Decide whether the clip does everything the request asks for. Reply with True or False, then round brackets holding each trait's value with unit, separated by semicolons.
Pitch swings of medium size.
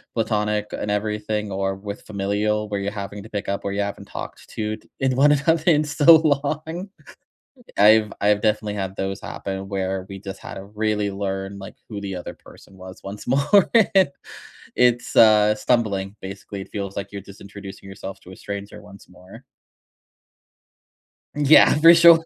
False (2.2 semitones)